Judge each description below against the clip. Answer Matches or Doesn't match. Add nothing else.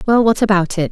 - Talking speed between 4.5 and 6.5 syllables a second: Matches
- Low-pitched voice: Doesn't match